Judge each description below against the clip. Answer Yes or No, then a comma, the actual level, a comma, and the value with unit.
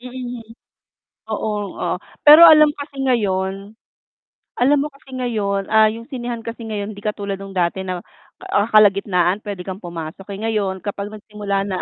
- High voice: Yes, high, 210 Hz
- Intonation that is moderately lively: Yes, average, 3.6 semitones